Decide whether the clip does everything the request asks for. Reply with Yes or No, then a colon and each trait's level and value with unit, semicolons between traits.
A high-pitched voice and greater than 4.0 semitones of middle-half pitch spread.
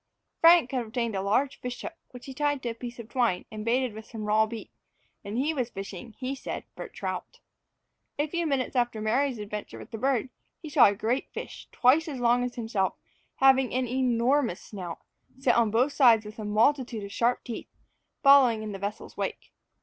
No: high, 240 Hz; average, 3.4 semitones